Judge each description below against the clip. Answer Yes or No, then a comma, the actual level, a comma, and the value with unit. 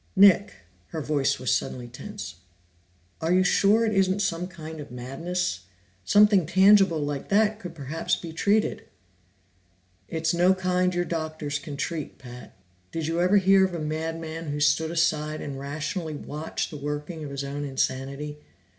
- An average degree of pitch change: Yes, average, 4.0 semitones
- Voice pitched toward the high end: No, medium, 160 Hz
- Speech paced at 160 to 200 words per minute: Yes, average, 165 wpm